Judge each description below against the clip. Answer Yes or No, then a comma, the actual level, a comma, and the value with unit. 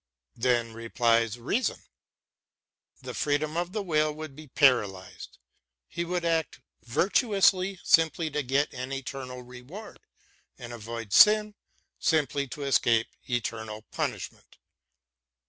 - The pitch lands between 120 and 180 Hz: Yes, medium, 140 Hz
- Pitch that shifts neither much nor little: No, wide, 5.7 semitones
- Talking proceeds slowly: Yes, slow, 115 wpm